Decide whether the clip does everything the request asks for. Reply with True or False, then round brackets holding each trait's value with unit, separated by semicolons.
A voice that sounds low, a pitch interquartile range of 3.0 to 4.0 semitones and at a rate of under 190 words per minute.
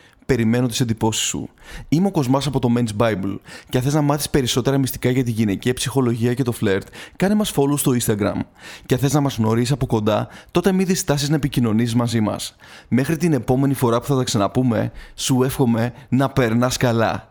False (125 Hz; 3.5 semitones; 200 wpm)